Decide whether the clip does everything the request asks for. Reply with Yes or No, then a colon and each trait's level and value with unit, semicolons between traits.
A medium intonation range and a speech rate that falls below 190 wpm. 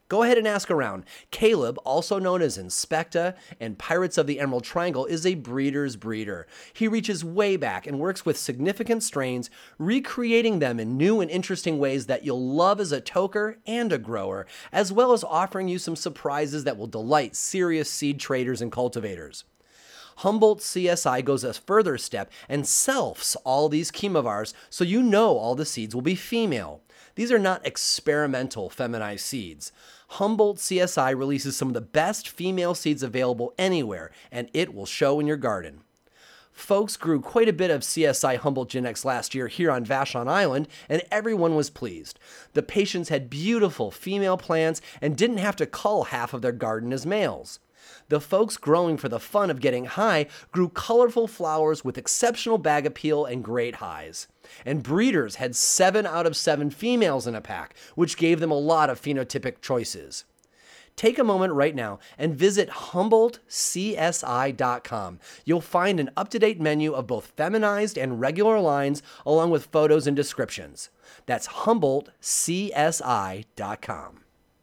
No: wide, 6.7 semitones; average, 165 wpm